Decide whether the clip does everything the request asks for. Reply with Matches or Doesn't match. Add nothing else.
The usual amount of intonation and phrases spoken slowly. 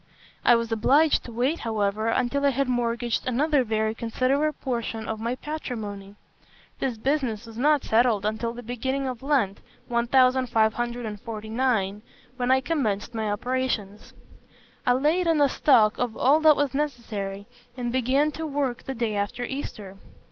Doesn't match